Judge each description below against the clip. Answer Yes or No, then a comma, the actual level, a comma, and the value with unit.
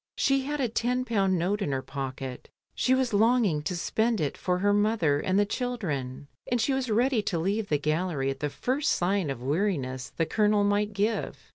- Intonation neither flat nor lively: No, wide, 7.3 semitones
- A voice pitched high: Yes, high, 200 Hz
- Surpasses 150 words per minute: Yes, fast, 205 wpm